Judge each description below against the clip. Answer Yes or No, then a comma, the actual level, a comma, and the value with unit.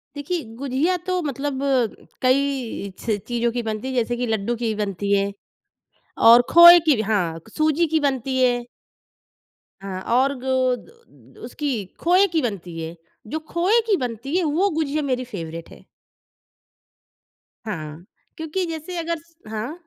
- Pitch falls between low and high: No, very high, 260 Hz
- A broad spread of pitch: Yes, wide, 6.6 semitones